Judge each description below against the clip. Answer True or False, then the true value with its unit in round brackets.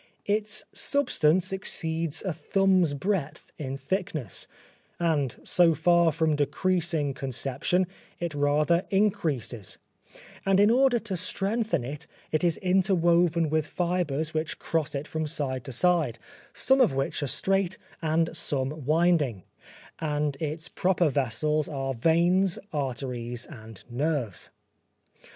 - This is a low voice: False (160 Hz)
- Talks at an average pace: False (125 wpm)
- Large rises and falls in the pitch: False (4.3 semitones)